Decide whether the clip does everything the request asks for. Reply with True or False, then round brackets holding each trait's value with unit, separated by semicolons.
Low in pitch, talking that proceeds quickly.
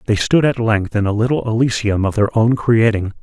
True (110 Hz; 225 wpm)